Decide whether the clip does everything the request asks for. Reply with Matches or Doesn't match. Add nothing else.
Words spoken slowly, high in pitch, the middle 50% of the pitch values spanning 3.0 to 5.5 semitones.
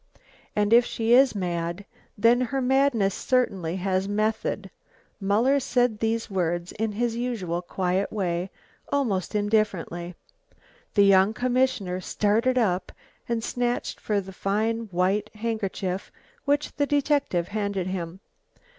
Matches